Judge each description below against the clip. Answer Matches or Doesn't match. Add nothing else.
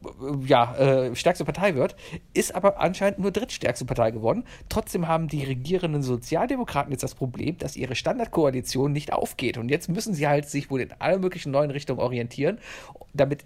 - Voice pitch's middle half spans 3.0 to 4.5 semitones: Doesn't match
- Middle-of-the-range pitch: Matches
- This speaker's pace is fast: Doesn't match